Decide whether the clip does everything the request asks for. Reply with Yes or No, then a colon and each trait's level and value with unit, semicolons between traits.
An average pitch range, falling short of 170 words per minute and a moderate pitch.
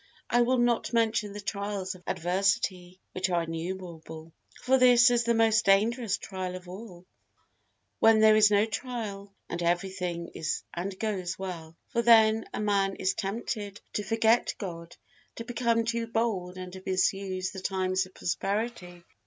No: average, 3.6 semitones; average, 160 wpm; high, 195 Hz